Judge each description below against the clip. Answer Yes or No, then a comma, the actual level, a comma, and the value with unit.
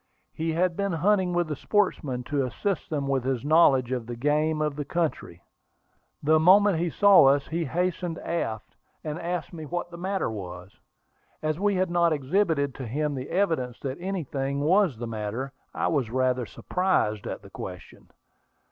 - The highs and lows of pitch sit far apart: No, average, 5.0 semitones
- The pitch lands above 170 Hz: No, medium, 155 Hz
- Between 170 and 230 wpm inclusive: Yes, average, 175 wpm